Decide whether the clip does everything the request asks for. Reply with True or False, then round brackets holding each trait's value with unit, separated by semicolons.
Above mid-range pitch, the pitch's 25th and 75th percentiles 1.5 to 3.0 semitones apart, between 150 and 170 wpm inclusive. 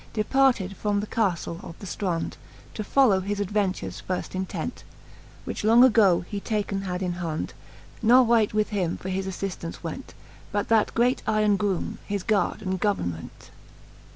True (200 Hz; 2.6 semitones; 160 wpm)